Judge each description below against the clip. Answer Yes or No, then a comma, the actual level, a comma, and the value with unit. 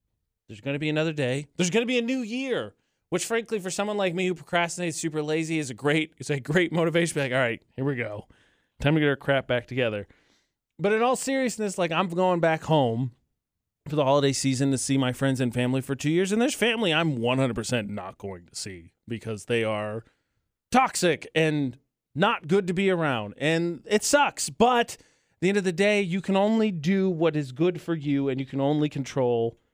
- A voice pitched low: No, medium, 155 Hz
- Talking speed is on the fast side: Yes, fast, 220 wpm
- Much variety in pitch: Yes, wide, 6.4 semitones